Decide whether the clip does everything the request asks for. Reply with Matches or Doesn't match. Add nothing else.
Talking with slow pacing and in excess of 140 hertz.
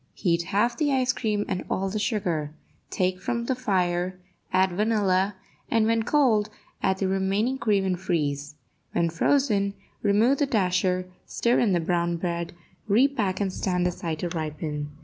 Doesn't match